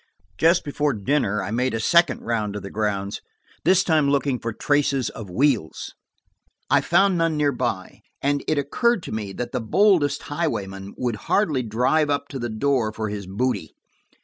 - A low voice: Yes, low, 130 Hz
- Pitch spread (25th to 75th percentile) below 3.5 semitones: No, wide, 5.6 semitones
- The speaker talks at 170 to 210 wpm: Yes, average, 175 wpm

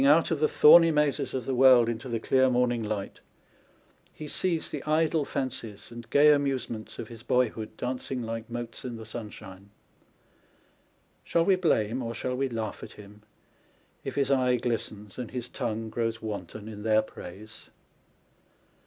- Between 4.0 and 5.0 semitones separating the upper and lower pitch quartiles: No, average, 3.5 semitones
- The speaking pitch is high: No, low, 120 Hz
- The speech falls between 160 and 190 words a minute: Yes, average, 170 wpm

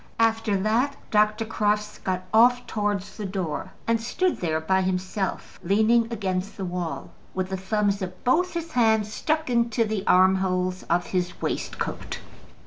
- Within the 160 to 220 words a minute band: No, average, 150 wpm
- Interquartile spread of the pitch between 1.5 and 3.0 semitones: No, average, 3.4 semitones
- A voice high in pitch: Yes, high, 210 Hz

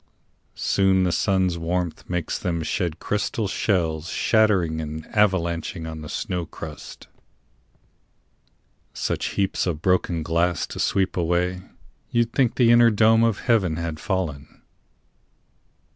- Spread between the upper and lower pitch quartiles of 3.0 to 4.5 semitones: Yes, average, 3.3 semitones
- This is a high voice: No, very low, 90 Hz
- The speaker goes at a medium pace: No, slow, 125 wpm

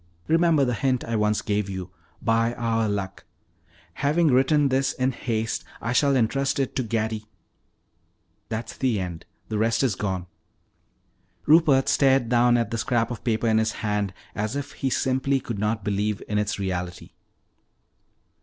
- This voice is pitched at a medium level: No, low, 115 Hz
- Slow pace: No, average, 165 wpm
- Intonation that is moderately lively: Yes, average, 3.9 semitones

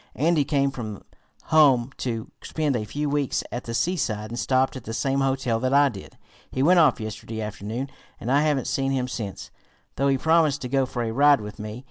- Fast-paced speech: Yes, fast, 210 wpm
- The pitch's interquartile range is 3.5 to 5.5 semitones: Yes, average, 3.8 semitones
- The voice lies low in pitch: Yes, low, 130 Hz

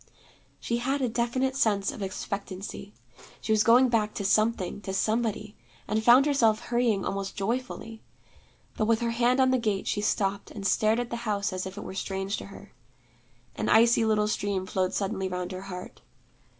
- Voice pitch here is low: No, high, 215 Hz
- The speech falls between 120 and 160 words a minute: No, average, 185 wpm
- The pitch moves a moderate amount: Yes, average, 3.2 semitones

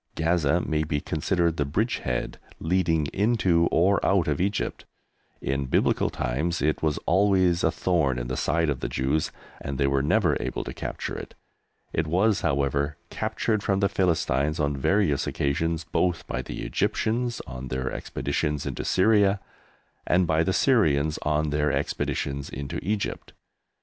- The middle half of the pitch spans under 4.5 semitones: No, average, 4.8 semitones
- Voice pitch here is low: Yes, very low, 80 Hz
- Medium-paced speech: Yes, average, 155 wpm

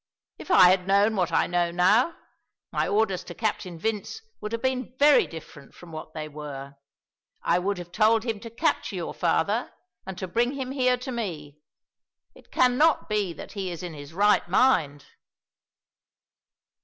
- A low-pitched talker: No, high, 195 Hz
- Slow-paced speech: No, average, 170 wpm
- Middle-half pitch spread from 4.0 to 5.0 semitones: No, wide, 5.4 semitones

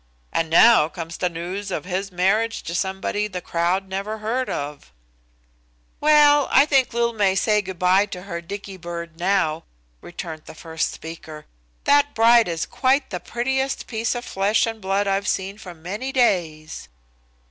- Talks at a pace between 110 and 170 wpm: Yes, average, 165 wpm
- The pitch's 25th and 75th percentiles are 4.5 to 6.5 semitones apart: Yes, average, 4.9 semitones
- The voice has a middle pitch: No, high, 195 Hz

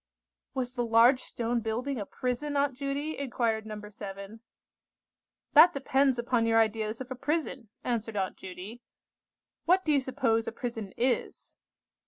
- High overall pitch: Yes, high, 240 Hz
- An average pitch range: Yes, average, 3.4 semitones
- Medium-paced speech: Yes, average, 150 wpm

